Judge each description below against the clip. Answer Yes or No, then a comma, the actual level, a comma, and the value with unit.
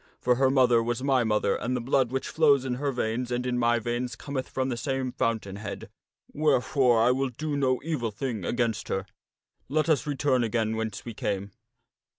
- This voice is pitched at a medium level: No, low, 125 Hz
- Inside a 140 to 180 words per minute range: No, average, 195 wpm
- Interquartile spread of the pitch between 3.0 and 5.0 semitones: No, narrow, 2.6 semitones